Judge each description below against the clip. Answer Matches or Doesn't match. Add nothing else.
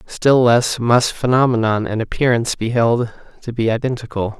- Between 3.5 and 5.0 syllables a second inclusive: Matches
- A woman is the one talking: Doesn't match